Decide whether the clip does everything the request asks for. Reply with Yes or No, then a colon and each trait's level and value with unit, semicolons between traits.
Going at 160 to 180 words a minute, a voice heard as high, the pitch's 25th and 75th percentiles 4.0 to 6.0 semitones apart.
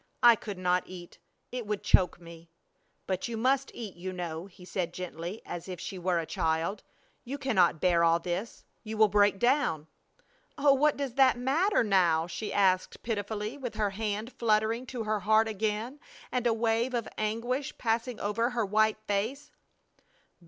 Yes: average, 175 wpm; high, 215 Hz; average, 4.6 semitones